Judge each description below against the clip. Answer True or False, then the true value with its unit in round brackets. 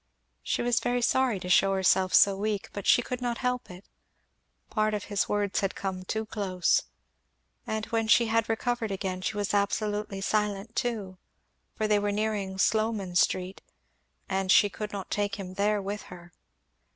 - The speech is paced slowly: False (175 wpm)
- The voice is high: True (205 Hz)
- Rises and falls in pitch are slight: True (2.2 semitones)